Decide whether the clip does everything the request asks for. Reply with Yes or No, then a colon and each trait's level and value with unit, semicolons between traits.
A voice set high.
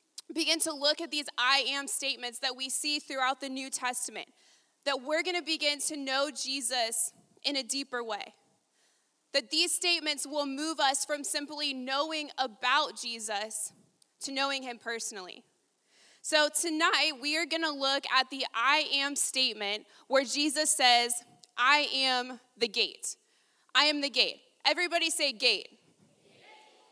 Yes: very high, 280 Hz